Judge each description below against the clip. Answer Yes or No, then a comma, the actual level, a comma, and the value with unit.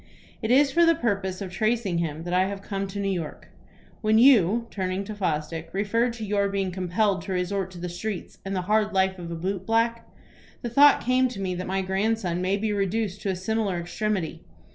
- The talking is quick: Yes, fast, 215 wpm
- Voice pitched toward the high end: Yes, high, 195 Hz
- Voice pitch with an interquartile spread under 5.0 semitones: Yes, average, 3.1 semitones